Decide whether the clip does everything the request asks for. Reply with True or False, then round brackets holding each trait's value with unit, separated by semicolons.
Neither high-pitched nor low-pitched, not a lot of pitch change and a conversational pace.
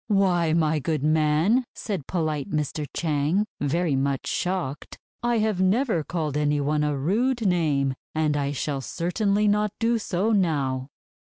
False (160 Hz; 5.2 semitones; 150 wpm)